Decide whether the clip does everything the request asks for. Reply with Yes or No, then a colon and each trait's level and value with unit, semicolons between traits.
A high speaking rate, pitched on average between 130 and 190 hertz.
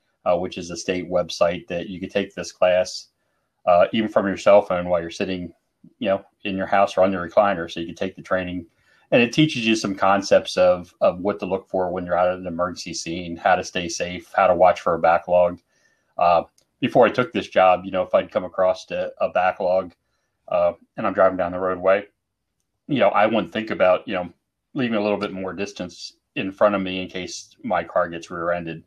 No: fast, 230 wpm; very low, 95 Hz